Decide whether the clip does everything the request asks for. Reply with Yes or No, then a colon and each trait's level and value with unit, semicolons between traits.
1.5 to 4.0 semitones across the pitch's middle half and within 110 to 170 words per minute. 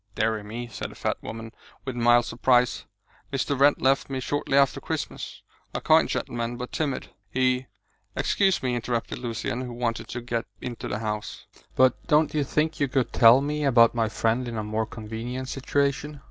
No: average, 2.9 semitones; average, 185 wpm